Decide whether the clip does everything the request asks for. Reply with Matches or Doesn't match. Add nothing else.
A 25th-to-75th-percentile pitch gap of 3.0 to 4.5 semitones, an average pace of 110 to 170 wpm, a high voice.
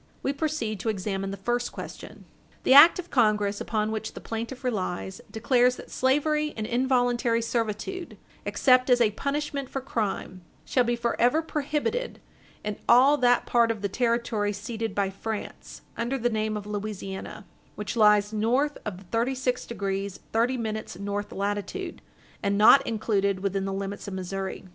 Matches